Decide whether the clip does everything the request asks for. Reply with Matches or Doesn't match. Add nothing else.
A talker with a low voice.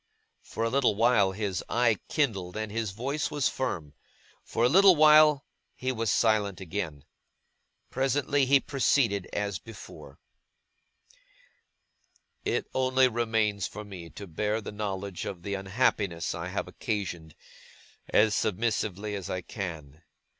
Matches